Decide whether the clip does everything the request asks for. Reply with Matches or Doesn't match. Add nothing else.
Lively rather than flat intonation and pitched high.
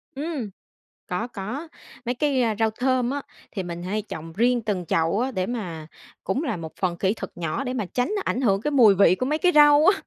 Matches